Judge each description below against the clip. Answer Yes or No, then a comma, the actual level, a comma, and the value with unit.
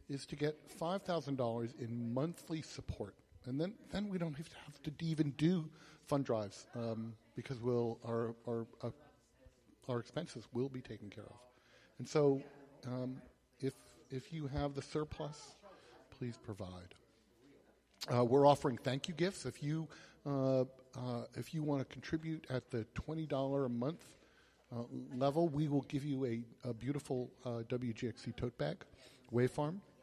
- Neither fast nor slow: Yes, average, 160 wpm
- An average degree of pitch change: Yes, average, 3.8 semitones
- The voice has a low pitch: Yes, low, 130 Hz